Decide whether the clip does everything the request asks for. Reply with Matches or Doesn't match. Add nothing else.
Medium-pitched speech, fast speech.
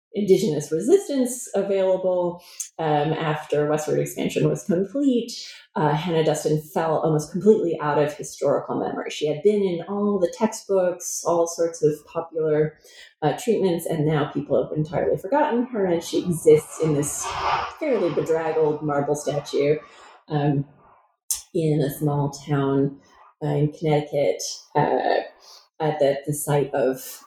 Doesn't match